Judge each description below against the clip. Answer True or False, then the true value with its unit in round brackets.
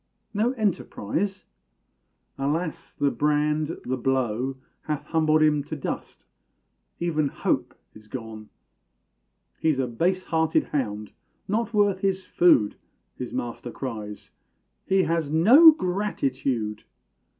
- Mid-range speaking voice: True (150 Hz)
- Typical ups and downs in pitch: False (6.3 semitones)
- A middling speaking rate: False (110 wpm)